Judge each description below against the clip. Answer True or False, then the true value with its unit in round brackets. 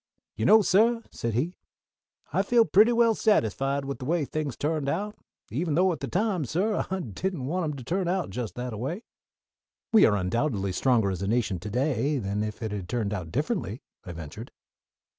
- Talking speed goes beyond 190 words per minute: True (200 wpm)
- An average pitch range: False (9.0 semitones)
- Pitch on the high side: False (140 Hz)